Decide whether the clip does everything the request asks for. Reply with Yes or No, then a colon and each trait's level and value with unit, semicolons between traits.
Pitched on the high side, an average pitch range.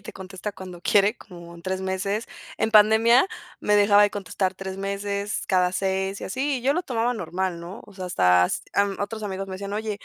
No: high, 200 Hz; narrow, 1.9 semitones